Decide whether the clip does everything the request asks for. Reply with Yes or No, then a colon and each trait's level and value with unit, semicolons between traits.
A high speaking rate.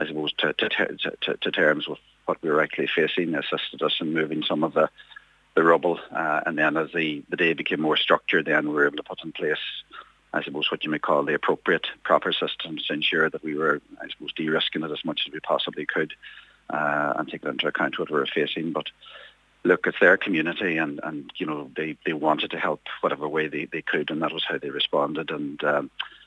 Yes: fast, 235 wpm